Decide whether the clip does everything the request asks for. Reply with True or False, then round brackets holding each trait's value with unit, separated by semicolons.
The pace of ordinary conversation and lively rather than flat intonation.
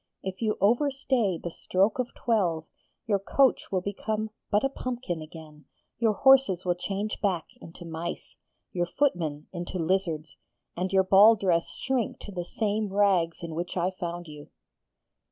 False (160 wpm; 3.9 semitones)